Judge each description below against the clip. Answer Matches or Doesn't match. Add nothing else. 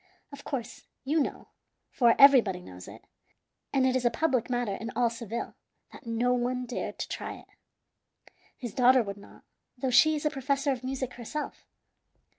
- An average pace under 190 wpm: Matches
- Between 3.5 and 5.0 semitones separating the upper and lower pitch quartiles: Doesn't match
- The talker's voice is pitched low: Doesn't match